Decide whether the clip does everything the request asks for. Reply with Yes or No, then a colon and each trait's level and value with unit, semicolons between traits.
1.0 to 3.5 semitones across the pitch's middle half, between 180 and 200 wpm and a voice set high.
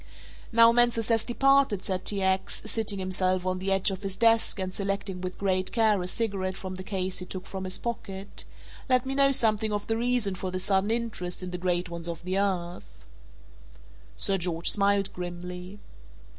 Yes: average, 3.2 semitones; average, 190 wpm; high, 195 Hz